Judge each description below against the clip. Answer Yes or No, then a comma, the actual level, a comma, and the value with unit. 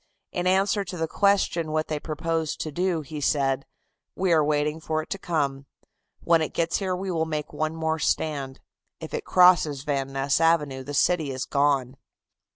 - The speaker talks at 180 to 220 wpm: Yes, average, 190 wpm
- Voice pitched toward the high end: No, medium, 155 Hz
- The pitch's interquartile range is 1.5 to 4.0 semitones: Yes, average, 2.9 semitones